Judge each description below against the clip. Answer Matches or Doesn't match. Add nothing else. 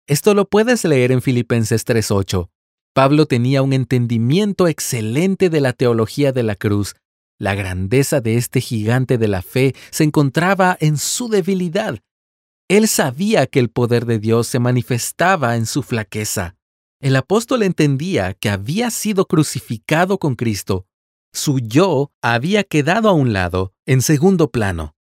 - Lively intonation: Matches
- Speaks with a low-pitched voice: Matches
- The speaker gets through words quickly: Doesn't match